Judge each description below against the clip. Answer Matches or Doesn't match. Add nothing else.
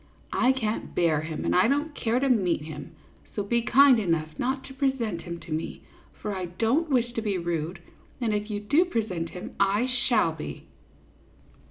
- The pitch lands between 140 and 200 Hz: Doesn't match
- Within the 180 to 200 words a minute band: Matches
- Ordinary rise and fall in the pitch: Doesn't match